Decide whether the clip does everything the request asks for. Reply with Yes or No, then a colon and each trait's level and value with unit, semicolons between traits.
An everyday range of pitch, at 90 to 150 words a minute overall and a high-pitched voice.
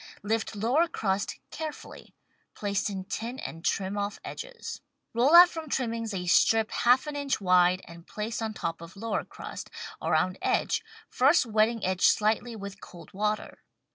No: average, 4.3 semitones; average, 160 wpm; high, 215 Hz